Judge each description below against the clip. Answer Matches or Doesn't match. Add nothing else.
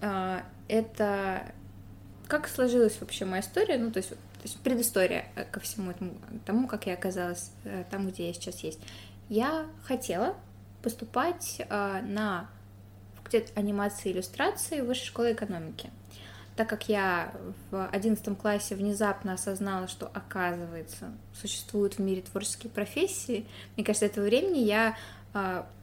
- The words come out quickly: Doesn't match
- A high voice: Matches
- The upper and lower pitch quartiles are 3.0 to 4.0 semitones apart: Doesn't match